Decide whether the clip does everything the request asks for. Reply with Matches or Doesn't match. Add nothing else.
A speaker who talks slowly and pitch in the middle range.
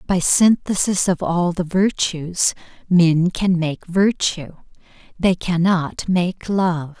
Matches